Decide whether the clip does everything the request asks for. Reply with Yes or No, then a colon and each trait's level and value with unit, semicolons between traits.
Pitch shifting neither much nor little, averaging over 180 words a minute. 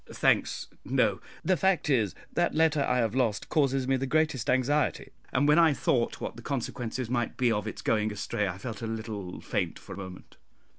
Yes: average, 4.6 semitones; average, 200 wpm